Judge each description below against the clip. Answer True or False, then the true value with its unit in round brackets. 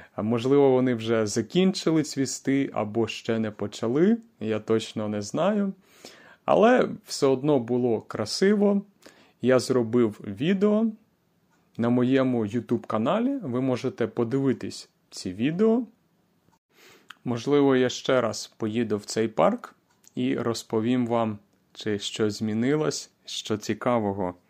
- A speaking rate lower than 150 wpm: True (110 wpm)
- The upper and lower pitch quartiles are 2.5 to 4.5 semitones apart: False (5.2 semitones)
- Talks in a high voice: False (125 Hz)